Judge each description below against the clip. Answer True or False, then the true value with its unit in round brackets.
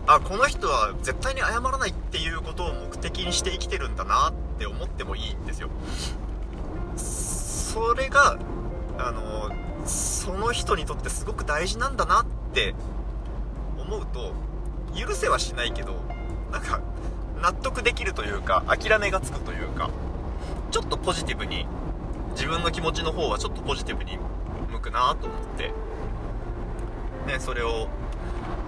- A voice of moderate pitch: False (80 Hz)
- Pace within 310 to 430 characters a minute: False (290 characters per minute)